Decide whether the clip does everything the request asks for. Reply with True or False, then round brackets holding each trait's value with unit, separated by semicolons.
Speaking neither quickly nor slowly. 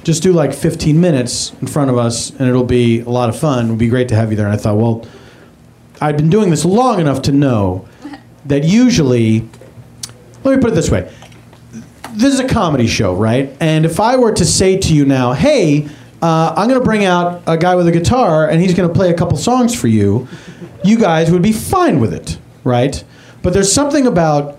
False (225 wpm)